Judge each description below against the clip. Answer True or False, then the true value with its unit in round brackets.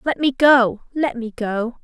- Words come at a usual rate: True (195 wpm)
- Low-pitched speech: False (245 Hz)